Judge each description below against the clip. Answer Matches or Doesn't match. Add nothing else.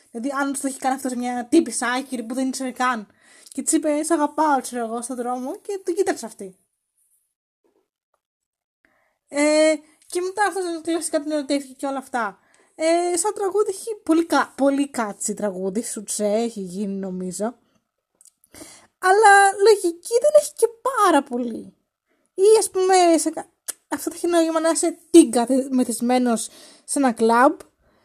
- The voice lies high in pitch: Matches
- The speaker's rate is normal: Matches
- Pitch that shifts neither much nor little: Doesn't match